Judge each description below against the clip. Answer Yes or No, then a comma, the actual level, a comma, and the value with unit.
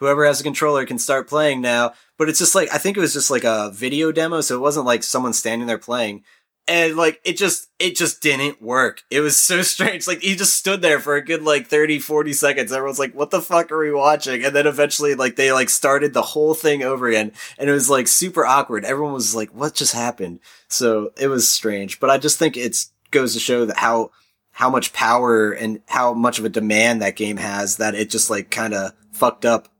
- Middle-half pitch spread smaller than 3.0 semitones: No, average, 4.6 semitones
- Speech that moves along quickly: Yes, fast, 240 wpm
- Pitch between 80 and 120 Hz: No, medium, 140 Hz